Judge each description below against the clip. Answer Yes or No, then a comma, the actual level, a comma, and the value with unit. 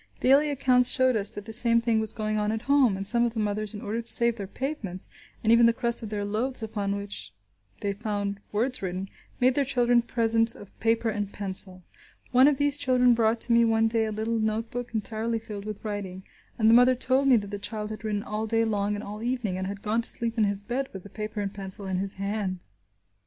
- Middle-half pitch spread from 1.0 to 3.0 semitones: Yes, narrow, 2.6 semitones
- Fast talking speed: Yes, fast, 240 wpm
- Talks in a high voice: Yes, high, 220 Hz